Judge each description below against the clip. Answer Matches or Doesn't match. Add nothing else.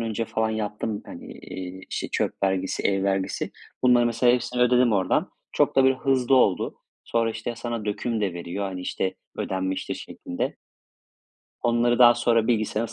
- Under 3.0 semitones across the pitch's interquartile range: Doesn't match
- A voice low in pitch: Matches